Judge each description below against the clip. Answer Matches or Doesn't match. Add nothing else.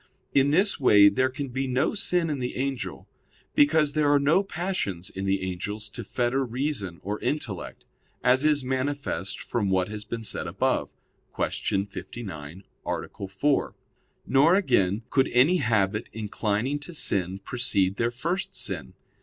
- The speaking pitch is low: Matches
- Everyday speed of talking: Matches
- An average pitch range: Doesn't match